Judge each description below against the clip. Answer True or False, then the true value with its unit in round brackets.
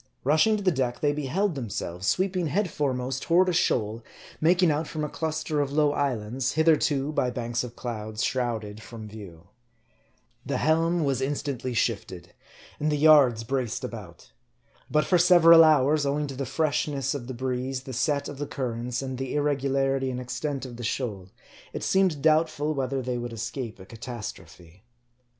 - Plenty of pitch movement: False (4.1 semitones)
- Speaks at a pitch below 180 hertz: True (135 Hz)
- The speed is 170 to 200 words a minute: True (175 wpm)